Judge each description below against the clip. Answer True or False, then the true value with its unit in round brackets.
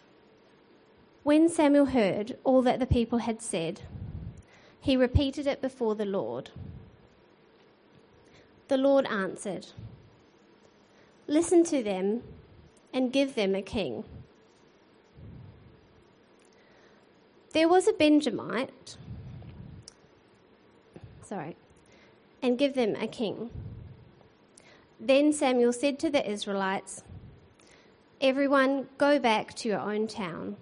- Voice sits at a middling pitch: False (260 Hz)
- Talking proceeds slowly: True (95 wpm)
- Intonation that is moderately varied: True (4.9 semitones)